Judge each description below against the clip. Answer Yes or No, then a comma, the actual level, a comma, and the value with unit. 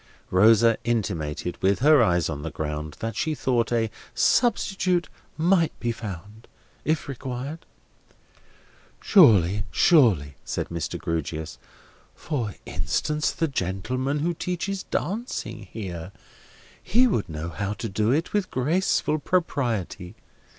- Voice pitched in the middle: No, low, 115 Hz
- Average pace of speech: No, slow, 115 wpm